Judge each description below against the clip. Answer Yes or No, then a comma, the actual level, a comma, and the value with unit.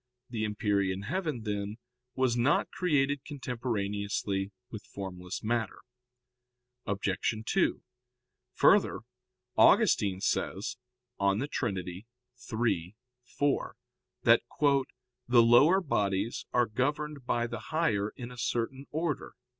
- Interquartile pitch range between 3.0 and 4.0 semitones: No, average, 4.6 semitones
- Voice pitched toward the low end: Yes, low, 115 Hz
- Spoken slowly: Yes, slow, 100 wpm